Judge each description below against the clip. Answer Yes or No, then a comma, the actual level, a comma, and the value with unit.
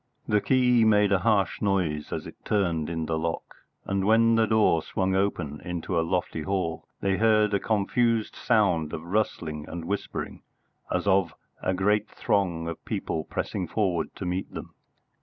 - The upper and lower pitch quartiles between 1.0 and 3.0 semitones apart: No, average, 4.1 semitones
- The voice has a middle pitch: No, very low, 95 Hz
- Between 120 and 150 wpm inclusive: No, average, 170 wpm